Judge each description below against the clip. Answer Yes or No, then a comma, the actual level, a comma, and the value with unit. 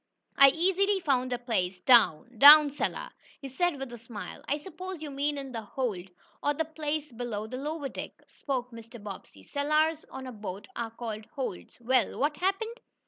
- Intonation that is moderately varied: Yes, average, 4.8 semitones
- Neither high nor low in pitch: No, very high, 270 Hz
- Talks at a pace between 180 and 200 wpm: Yes, average, 185 wpm